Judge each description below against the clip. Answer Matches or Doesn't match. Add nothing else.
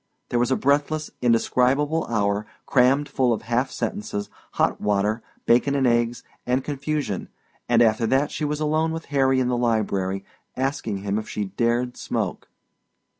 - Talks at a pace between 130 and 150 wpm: Doesn't match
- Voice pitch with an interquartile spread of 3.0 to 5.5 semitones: Matches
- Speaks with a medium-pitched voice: Doesn't match